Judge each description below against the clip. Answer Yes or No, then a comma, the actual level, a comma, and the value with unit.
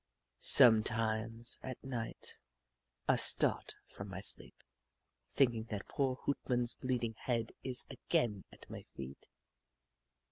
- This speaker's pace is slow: Yes, slow, 115 wpm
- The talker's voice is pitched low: Yes, low, 115 Hz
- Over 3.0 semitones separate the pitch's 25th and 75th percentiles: No, narrow, 2.6 semitones